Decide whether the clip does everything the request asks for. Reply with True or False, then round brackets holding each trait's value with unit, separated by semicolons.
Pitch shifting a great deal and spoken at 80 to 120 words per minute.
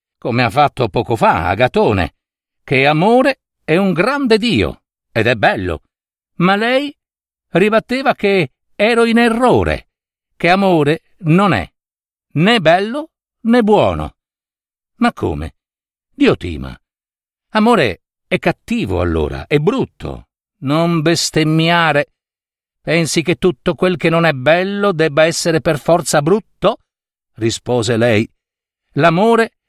True (6.2 semitones; 115 wpm)